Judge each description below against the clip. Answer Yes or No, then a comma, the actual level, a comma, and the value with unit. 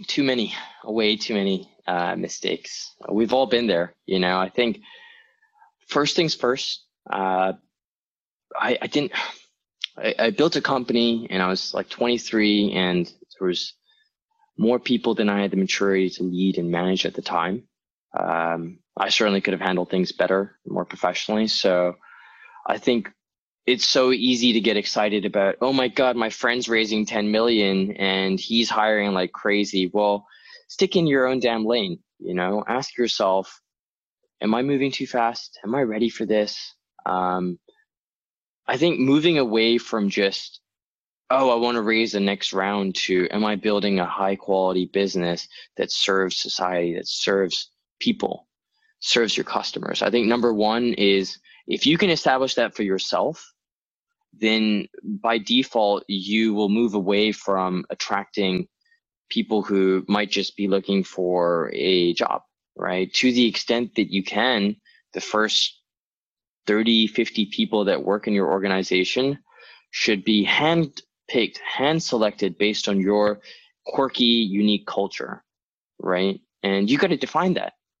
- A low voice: Yes, low, 105 Hz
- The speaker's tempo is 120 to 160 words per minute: Yes, average, 155 wpm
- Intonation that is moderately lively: Yes, average, 3.9 semitones